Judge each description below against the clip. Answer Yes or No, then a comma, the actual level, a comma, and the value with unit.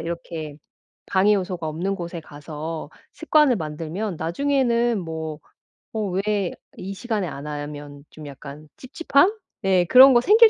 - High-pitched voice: No, medium, 180 Hz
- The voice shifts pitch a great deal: Yes, wide, 6.1 semitones